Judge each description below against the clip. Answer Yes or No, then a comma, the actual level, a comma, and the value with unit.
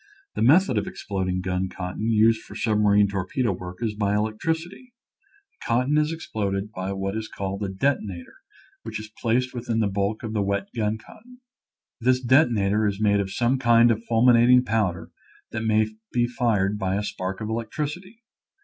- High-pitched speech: No, low, 110 Hz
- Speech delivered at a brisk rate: No, average, 175 wpm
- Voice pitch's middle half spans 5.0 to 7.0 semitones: No, average, 3.5 semitones